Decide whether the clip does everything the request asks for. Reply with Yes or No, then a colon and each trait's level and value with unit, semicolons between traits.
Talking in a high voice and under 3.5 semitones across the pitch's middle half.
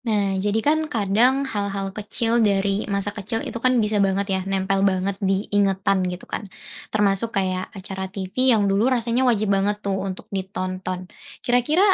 Yes: high, 200 Hz; narrow, 2.6 semitones